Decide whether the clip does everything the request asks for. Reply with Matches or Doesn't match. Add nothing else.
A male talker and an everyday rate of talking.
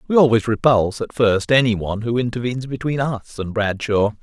Matches